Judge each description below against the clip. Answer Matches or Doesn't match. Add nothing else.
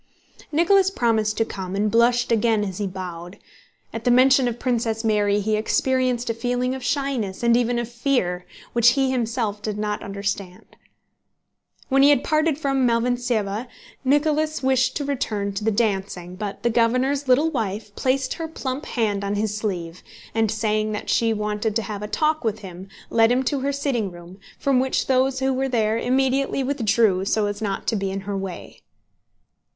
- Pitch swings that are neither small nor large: Matches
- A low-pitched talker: Doesn't match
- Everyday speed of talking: Matches